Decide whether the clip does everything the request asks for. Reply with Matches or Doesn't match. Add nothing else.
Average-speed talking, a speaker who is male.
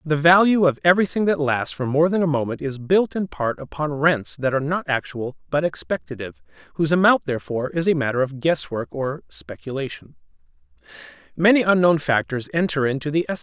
Matches